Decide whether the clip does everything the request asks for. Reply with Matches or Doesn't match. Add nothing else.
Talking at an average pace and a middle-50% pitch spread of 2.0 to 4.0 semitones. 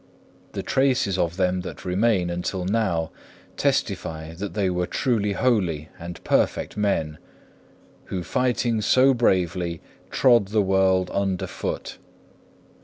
Doesn't match